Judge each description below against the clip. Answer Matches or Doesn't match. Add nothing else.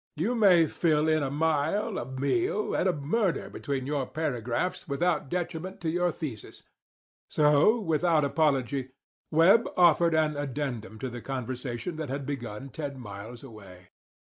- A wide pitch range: Doesn't match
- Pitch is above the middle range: Doesn't match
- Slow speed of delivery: Doesn't match